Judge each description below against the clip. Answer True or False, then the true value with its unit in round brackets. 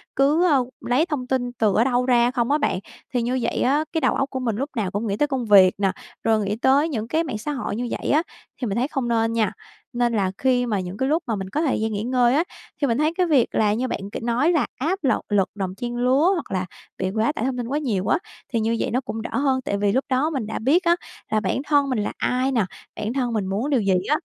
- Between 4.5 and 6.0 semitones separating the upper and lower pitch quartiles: False (4.1 semitones)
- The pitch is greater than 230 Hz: True (245 Hz)